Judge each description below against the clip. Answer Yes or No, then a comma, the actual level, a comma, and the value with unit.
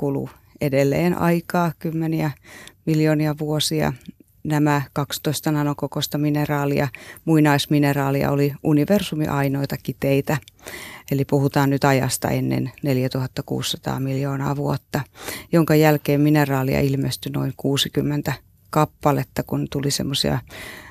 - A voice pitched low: No, medium, 145 Hz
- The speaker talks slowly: Yes, slow, 90 wpm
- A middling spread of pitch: No, narrow, 1.8 semitones